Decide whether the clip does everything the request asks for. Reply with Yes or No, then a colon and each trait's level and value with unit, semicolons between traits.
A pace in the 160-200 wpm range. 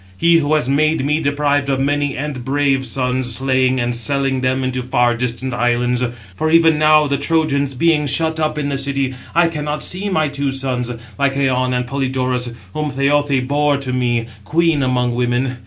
Yes: average, 180 wpm